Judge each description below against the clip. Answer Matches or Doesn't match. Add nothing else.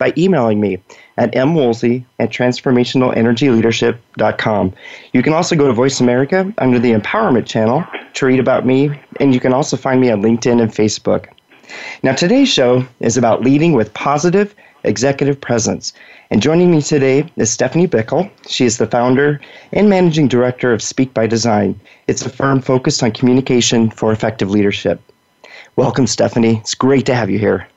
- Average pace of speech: Matches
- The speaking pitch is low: Matches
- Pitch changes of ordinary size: Matches